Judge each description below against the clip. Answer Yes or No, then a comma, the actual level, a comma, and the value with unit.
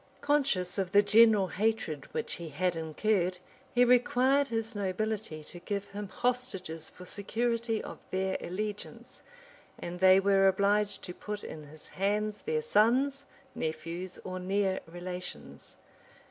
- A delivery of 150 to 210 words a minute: No, average, 140 wpm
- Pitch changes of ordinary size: Yes, average, 3.6 semitones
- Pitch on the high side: Yes, high, 200 Hz